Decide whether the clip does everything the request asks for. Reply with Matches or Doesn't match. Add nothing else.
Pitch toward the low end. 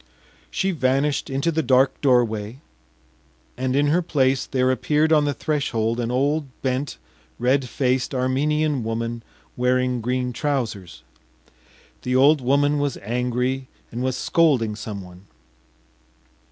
Matches